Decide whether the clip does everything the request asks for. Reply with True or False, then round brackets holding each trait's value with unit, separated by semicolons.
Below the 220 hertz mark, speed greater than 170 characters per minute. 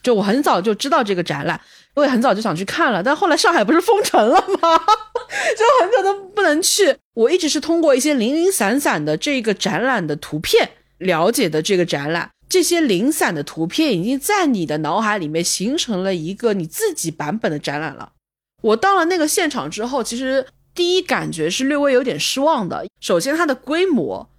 False (265 Hz; 305 characters per minute)